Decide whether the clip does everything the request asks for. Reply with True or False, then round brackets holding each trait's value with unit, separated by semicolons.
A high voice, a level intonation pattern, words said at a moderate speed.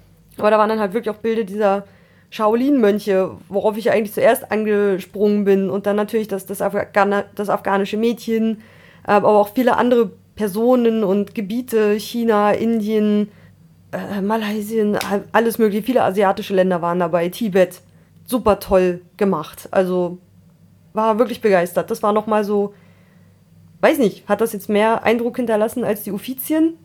True (210 Hz; 2.1 semitones; 145 wpm)